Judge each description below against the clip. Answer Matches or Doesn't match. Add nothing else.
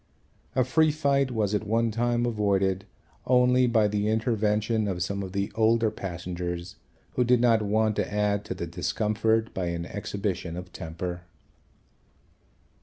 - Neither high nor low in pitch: Doesn't match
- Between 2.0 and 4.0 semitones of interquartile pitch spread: Matches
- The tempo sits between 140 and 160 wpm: Matches